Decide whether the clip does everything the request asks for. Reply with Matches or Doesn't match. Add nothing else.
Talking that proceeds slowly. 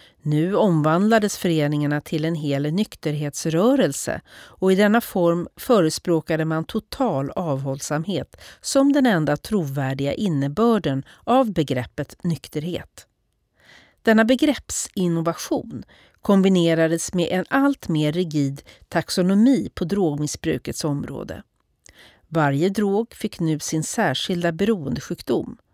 Matches